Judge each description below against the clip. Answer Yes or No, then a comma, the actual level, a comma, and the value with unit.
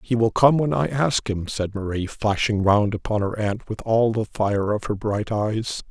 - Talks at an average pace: No, fast, 225 wpm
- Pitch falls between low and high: No, low, 110 Hz